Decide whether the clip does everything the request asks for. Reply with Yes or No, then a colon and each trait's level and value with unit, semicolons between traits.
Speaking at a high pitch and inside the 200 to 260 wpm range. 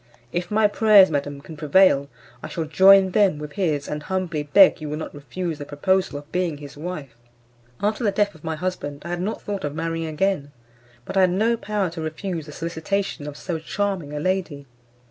No: medium, 165 Hz; fast, 205 wpm